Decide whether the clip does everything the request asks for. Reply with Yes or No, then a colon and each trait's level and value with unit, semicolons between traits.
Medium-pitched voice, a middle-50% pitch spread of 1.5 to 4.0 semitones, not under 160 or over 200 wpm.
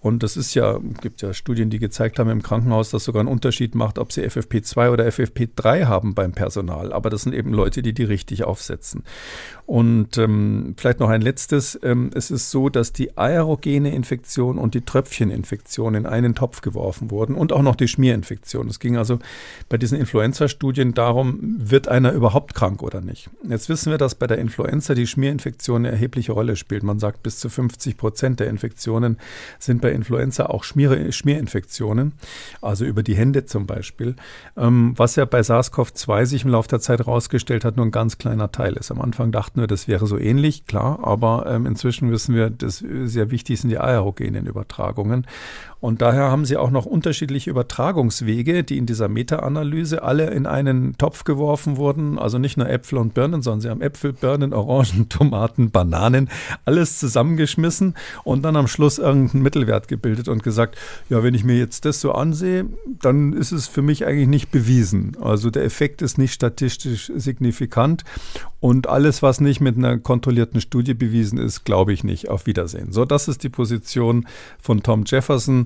No: low, 120 Hz; average, 3.3 semitones; average, 185 wpm